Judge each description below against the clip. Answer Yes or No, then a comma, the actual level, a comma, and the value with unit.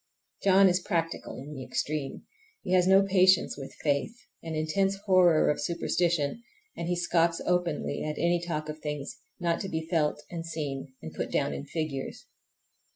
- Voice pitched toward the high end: No, medium, 165 Hz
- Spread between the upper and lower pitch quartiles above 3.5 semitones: No, average, 3.1 semitones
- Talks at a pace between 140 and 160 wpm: No, average, 170 wpm